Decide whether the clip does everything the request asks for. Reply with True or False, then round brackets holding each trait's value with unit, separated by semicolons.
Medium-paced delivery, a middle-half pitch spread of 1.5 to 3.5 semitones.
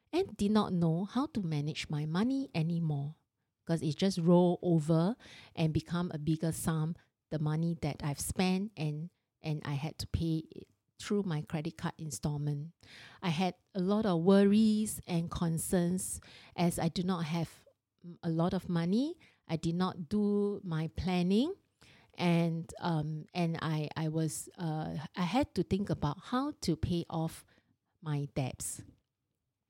True (160 wpm; 3.1 semitones)